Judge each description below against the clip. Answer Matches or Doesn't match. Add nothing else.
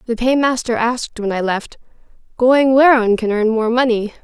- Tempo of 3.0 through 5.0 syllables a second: Doesn't match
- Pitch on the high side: Matches